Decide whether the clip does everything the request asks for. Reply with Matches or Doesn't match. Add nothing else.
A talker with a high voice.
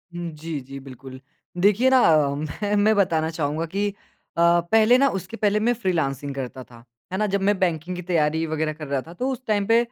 Doesn't match